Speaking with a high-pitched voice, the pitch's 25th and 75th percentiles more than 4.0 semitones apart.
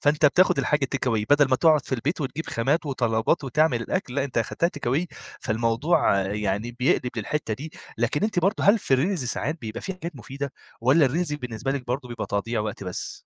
No: low, 135 Hz; average, 4.7 semitones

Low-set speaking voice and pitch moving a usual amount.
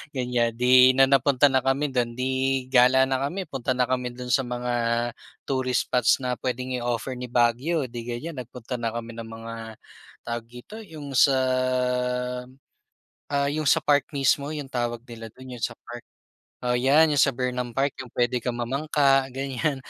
No: low, 130 Hz; narrow, 2.0 semitones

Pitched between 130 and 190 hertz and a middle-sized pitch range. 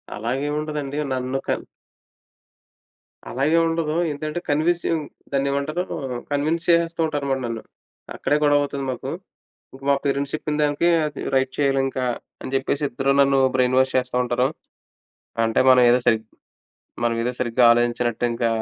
Yes: low, 135 Hz; average, 3.0 semitones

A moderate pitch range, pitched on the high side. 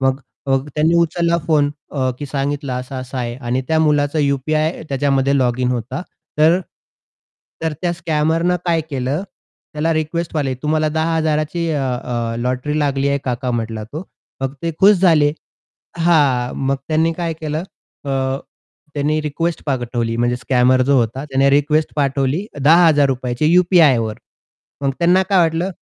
No: average, 3.6 semitones; medium, 145 Hz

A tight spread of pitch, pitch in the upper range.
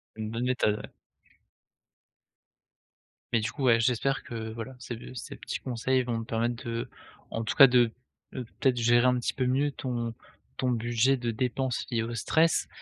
No: narrow, 1.9 semitones; low, 120 Hz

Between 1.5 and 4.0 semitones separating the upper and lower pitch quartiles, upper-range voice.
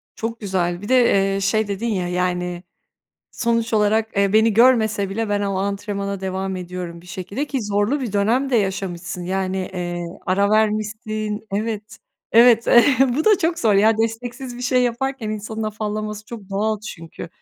Yes: average, 2.9 semitones; high, 210 Hz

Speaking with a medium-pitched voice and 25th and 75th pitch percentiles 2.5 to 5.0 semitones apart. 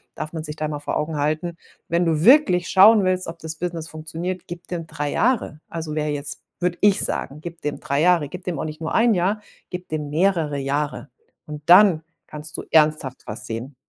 Yes: medium, 160 Hz; average, 2.9 semitones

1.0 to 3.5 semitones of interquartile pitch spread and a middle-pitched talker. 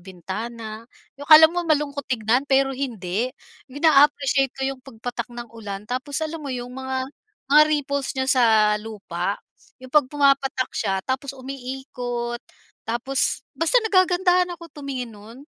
No: average, 3.1 semitones; very high, 260 Hz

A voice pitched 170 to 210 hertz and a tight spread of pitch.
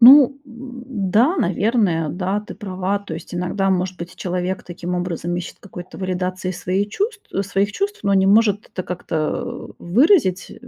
No: high, 190 Hz; average, 3.7 semitones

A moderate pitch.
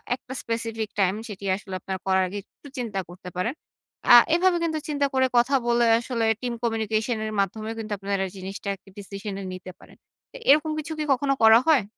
No: high, 225 Hz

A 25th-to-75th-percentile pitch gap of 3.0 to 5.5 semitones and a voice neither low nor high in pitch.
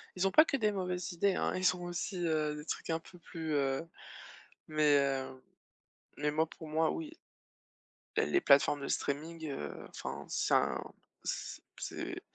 Yes: average, 3.7 semitones; medium, 160 Hz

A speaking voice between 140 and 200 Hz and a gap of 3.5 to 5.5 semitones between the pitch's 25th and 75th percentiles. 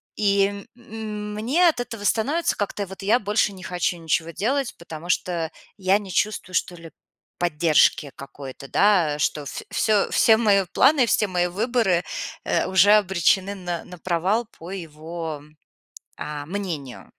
Yes: high, 190 Hz; average, 3.9 semitones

